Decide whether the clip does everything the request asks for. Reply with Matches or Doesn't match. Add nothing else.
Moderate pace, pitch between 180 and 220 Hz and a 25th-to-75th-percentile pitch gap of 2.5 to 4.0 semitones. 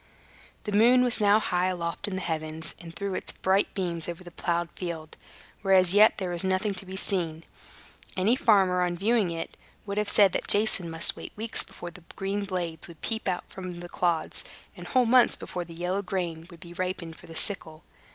Doesn't match